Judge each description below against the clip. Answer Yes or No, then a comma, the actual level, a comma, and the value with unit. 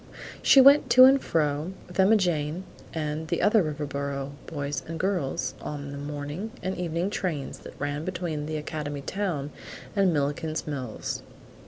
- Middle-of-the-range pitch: Yes, medium, 155 Hz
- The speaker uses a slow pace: No, average, 155 wpm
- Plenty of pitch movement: No, average, 4.2 semitones